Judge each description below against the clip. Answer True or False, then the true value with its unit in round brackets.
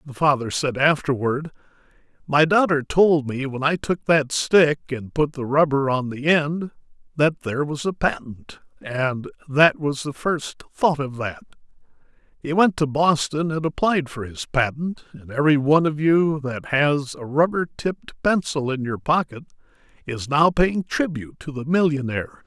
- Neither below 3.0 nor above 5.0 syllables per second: True (4.6 syllables/s)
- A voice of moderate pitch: True (150 Hz)